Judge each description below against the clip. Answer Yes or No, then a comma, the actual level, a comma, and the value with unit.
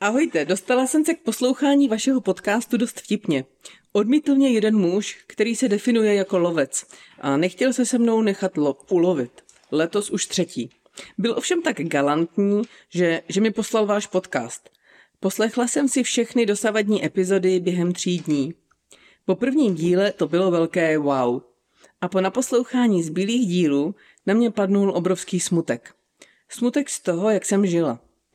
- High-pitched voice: Yes, high, 200 Hz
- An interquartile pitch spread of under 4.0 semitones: No, average, 5.2 semitones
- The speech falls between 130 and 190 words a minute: Yes, average, 150 wpm